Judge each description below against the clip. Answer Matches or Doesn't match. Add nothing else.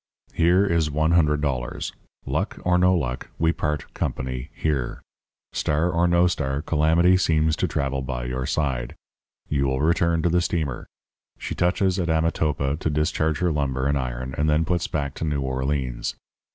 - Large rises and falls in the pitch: Doesn't match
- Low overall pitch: Matches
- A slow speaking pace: Doesn't match